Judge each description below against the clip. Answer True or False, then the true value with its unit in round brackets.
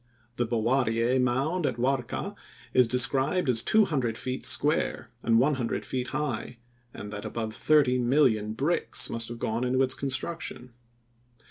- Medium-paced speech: True (150 wpm)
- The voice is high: False (125 Hz)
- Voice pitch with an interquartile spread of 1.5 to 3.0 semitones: True (2.7 semitones)